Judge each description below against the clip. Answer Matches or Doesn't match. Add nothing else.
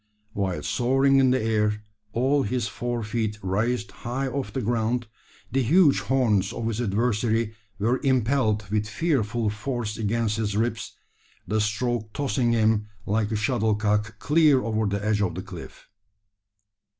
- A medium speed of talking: Matches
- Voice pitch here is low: Matches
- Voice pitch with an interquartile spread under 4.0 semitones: Matches